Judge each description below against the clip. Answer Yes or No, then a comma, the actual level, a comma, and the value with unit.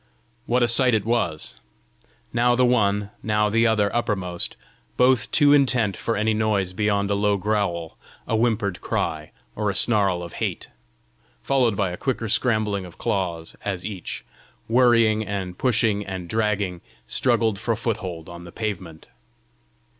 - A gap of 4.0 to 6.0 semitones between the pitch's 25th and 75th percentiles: No, average, 3.5 semitones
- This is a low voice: Yes, low, 105 Hz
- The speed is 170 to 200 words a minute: No, average, 150 wpm